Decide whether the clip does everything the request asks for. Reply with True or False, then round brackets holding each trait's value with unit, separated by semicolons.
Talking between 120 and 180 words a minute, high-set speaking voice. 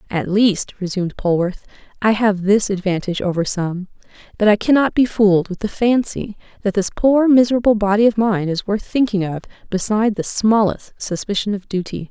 True (175 wpm; 205 Hz)